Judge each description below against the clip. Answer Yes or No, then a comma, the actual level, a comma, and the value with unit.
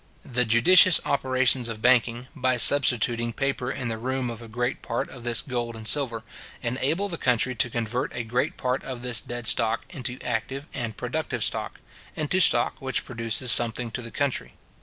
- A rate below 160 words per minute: No, average, 180 wpm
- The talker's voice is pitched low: Yes, low, 125 Hz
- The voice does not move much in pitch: Yes, narrow, 2.0 semitones